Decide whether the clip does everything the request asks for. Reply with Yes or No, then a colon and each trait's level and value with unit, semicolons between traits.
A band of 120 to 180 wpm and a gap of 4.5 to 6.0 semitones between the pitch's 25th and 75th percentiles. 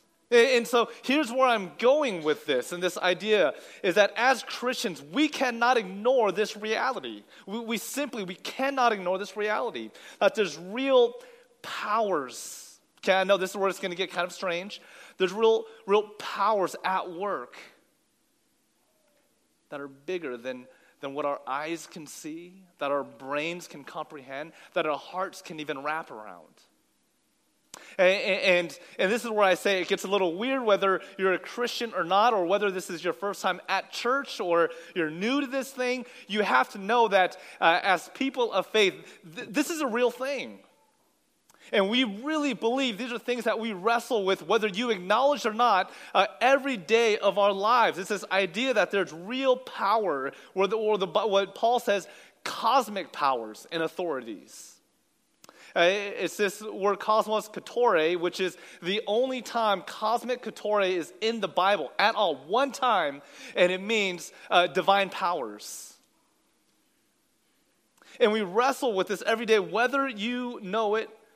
Yes: average, 170 wpm; average, 4.8 semitones